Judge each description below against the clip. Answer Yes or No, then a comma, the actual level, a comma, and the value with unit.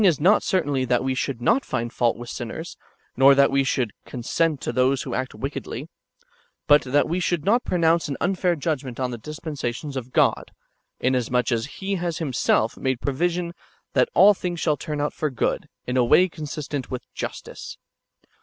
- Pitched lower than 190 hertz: Yes, medium, 140 Hz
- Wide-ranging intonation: No, average, 4.8 semitones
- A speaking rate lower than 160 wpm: No, average, 185 wpm